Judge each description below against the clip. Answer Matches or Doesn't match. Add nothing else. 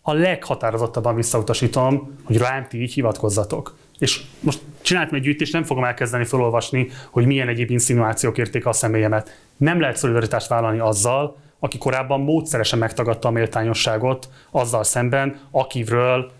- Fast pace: Doesn't match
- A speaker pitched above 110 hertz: Matches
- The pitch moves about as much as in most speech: Matches